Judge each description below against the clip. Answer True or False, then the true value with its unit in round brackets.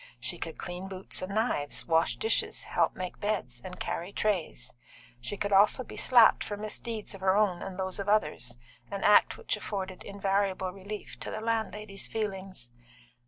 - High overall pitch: True (195 Hz)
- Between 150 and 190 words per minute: True (170 wpm)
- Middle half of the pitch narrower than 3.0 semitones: True (2.4 semitones)